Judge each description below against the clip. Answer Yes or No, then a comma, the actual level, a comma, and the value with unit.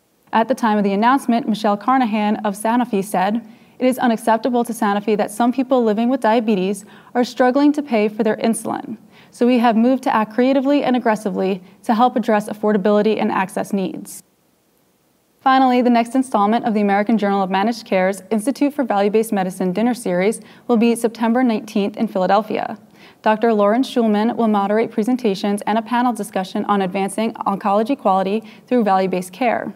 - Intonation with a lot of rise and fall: No, average, 3.0 semitones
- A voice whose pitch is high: Yes, high, 220 Hz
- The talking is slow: No, average, 170 wpm